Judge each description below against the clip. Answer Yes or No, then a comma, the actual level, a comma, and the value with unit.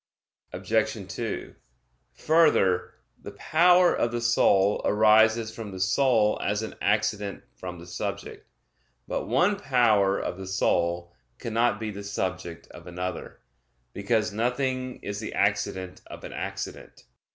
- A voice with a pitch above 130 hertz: No, low, 105 Hz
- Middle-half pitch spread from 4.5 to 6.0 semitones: No, average, 3.8 semitones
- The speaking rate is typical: No, slow, 130 wpm